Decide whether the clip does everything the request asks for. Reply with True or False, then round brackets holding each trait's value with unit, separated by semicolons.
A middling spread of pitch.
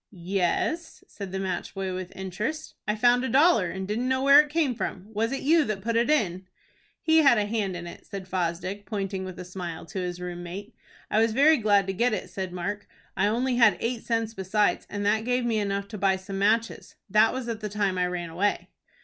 True (3.9 semitones)